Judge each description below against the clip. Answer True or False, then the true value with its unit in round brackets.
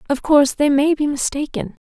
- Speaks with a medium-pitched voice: False (285 Hz)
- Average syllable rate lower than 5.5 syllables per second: False (5.6 syllables/s)